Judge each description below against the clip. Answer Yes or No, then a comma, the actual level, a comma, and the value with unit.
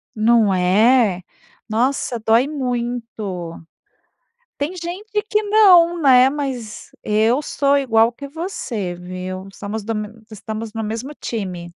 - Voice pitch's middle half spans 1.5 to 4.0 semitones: No, average, 4.9 semitones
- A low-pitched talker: No, high, 230 Hz